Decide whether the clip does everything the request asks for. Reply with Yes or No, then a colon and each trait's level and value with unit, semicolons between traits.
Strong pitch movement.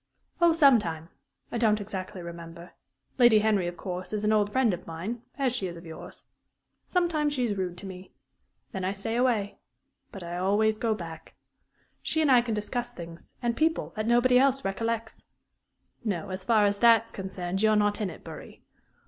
No: average, 4.4 semitones